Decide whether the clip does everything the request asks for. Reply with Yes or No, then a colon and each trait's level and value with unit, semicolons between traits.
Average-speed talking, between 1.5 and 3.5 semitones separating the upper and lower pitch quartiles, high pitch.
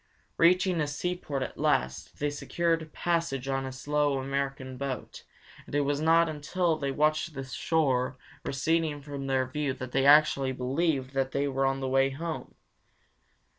No: average, 165 wpm; average, 2.7 semitones; medium, 140 Hz